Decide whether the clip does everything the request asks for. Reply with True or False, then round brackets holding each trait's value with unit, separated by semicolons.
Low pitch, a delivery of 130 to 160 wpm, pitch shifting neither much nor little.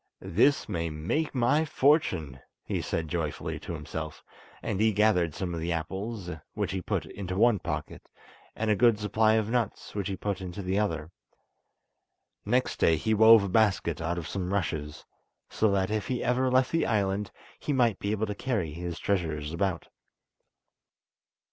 False (100 Hz; 175 wpm; 4.7 semitones)